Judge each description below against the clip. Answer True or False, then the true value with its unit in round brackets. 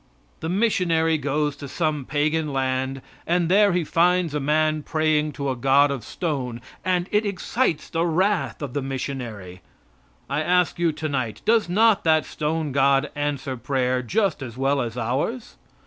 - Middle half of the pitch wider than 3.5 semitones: True (4.2 semitones)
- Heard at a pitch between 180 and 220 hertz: False (150 Hz)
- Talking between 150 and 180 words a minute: True (165 wpm)